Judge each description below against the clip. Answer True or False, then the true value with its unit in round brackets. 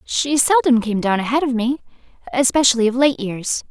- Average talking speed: True (180 wpm)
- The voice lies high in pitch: True (255 Hz)